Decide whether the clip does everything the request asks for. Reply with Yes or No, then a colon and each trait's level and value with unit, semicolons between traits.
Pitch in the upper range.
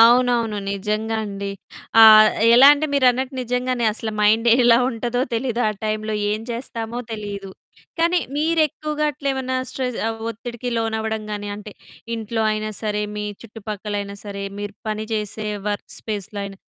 Yes: high, 220 Hz